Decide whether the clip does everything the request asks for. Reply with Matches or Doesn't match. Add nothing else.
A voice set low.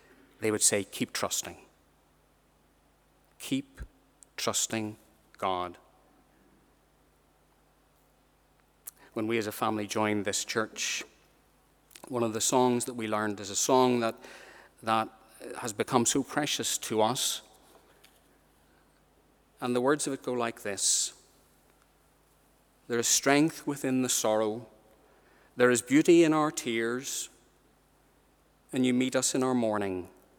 Matches